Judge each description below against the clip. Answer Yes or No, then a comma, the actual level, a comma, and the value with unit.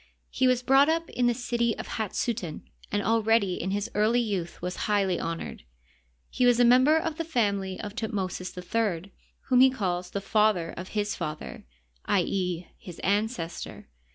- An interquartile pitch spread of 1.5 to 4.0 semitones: No, average, 4.7 semitones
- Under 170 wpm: No, average, 175 wpm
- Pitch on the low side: No, high, 210 Hz